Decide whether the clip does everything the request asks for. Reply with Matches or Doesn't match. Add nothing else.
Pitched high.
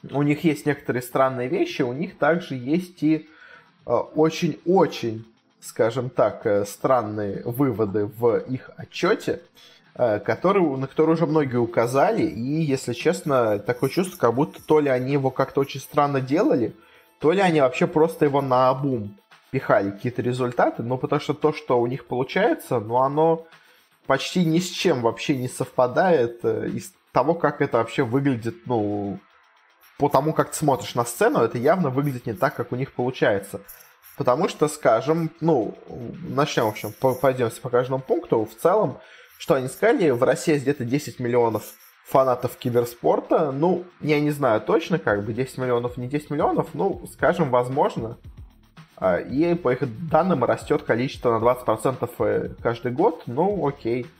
Doesn't match